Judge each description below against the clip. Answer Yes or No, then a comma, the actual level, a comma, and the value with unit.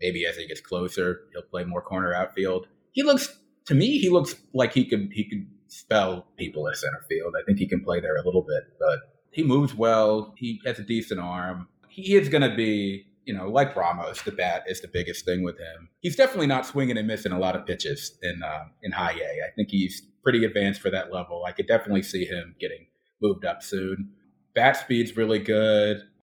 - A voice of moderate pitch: No, low, 110 Hz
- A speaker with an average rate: No, fast, 220 wpm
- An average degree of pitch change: No, wide, 8.6 semitones